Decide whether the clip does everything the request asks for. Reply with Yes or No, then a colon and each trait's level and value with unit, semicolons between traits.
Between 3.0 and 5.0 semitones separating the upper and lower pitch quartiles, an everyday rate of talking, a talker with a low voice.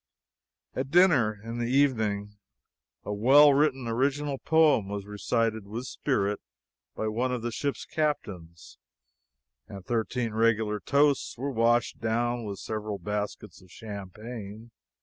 No: average, 4.1 semitones; slow, 130 wpm; low, 115 Hz